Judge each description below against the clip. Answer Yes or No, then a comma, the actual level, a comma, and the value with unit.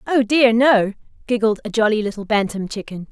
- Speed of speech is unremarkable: Yes, average, 175 wpm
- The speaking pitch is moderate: No, high, 225 Hz